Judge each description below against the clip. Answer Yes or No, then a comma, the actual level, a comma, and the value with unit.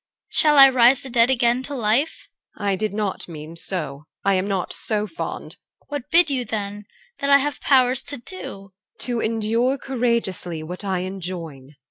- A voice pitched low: No, high, 220 Hz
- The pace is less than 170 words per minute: No, average, 185 wpm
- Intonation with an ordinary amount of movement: No, wide, 5.7 semitones